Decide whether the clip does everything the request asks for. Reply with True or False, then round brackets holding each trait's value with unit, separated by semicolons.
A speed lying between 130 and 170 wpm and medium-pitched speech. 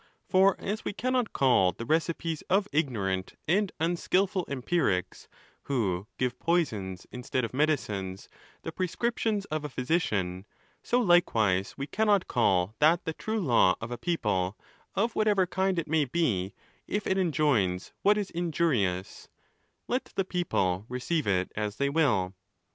True (150 wpm; 150 Hz)